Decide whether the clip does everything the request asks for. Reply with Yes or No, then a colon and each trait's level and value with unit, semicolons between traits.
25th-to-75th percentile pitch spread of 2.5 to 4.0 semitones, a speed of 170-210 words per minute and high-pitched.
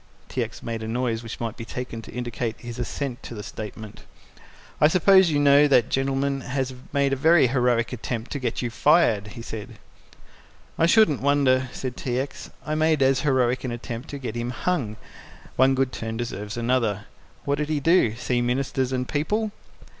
No: average, 3.3 semitones; average, 190 wpm; low, 130 Hz